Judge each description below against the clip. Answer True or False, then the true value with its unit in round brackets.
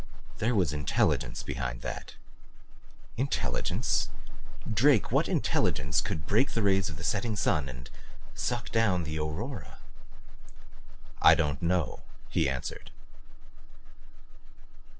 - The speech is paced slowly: True (110 wpm)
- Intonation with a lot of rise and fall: True (7.1 semitones)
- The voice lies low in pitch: True (90 Hz)